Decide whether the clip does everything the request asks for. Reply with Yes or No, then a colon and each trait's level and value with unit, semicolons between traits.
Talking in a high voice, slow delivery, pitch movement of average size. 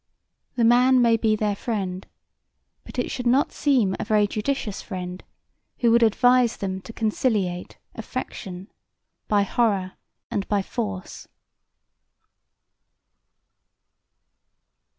Yes: high, 215 Hz; slow, 110 wpm; average, 3.7 semitones